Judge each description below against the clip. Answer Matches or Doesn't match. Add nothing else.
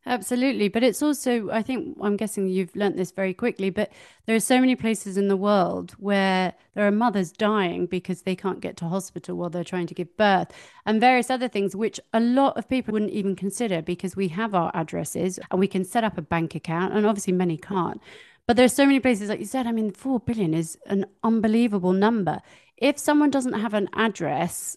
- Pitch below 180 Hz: Doesn't match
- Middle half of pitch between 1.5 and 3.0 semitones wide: Doesn't match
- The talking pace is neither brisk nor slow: Doesn't match